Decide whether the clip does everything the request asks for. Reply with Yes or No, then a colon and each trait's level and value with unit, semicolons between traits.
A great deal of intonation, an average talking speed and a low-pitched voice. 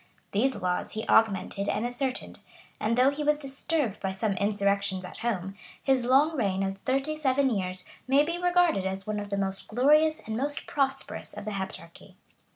No: wide, 5.9 semitones; average, 180 wpm; high, 225 Hz